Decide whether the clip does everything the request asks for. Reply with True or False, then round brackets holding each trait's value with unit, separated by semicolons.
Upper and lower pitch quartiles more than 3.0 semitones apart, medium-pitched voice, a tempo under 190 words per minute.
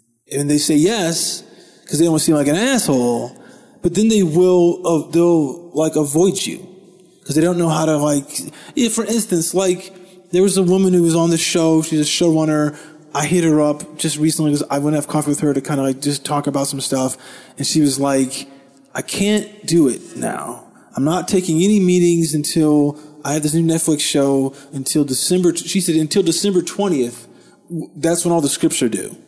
False (3.6 semitones; 160 Hz; 205 wpm)